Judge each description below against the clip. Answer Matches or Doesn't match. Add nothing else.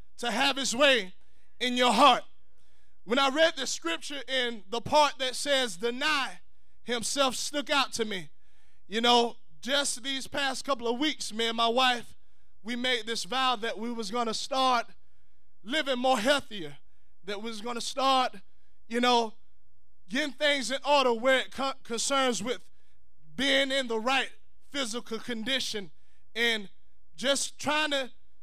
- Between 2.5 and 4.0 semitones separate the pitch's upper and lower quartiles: Matches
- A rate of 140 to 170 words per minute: Matches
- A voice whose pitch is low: Doesn't match